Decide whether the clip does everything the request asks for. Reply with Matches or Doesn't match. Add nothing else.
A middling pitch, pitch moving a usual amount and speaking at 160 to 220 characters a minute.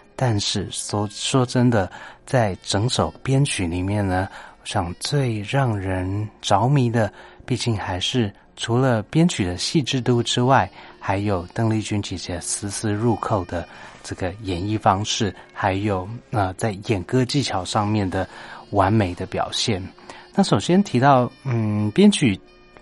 Doesn't match